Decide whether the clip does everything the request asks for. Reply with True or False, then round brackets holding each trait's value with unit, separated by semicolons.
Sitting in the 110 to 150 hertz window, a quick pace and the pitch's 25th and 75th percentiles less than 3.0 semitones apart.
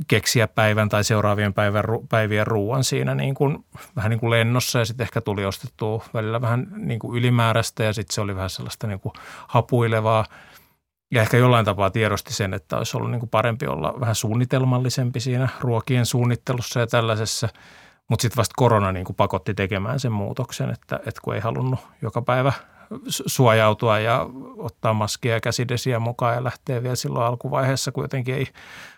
True (115 Hz; 170 wpm; 2.6 semitones)